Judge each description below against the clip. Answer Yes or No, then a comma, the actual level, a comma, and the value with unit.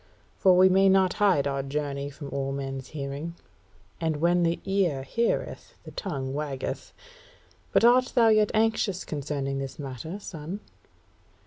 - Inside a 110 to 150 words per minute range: Yes, average, 145 wpm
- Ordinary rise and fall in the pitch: No, wide, 5.8 semitones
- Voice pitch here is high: No, medium, 155 Hz